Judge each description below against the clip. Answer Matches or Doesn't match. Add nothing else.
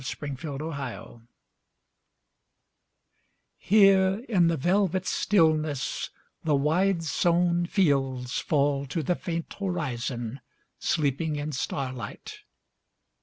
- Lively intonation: Doesn't match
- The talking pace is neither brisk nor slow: Doesn't match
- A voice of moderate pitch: Matches